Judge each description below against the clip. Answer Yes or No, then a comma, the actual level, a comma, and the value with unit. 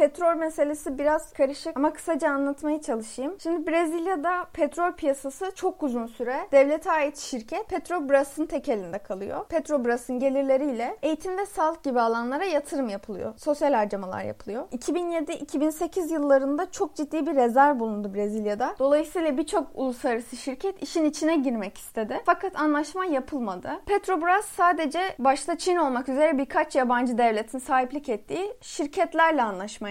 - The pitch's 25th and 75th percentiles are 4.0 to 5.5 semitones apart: Yes, average, 4.3 semitones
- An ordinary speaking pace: Yes, average, 130 wpm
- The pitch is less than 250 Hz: No, very high, 295 Hz